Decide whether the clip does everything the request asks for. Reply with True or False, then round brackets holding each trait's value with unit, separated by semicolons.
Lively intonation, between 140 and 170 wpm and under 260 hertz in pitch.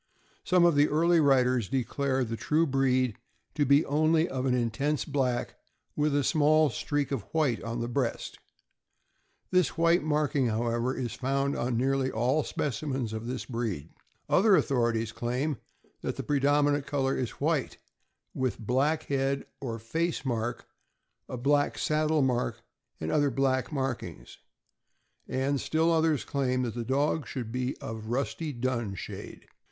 False (3.4 semitones; 150 wpm; 135 Hz)